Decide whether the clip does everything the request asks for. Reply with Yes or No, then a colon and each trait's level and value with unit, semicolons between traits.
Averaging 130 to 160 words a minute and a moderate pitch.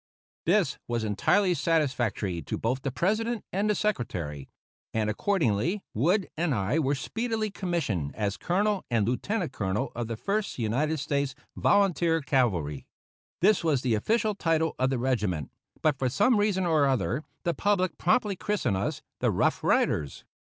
Yes: average, 150 wpm; medium, 145 Hz